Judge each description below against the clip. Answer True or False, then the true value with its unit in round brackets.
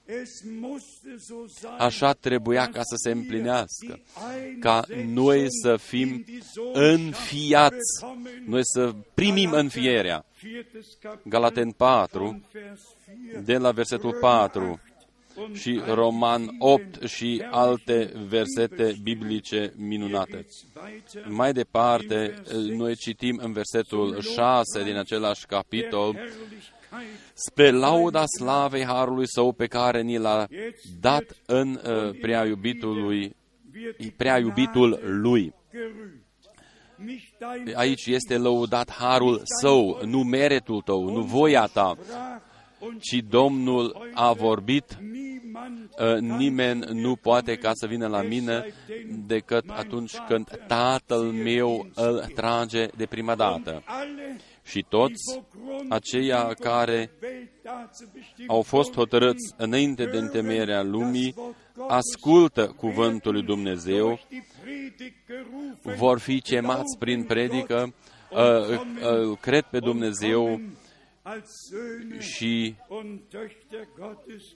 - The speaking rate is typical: False (95 wpm)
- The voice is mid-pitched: False (125 Hz)